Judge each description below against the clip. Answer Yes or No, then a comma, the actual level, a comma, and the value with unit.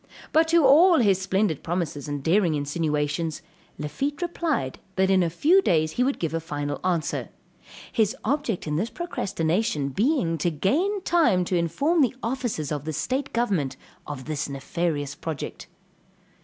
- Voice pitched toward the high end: No, medium, 180 Hz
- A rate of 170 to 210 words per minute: No, average, 155 wpm